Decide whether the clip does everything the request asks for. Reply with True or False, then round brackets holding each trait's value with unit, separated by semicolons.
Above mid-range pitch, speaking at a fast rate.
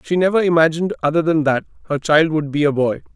False (155 Hz; 230 wpm)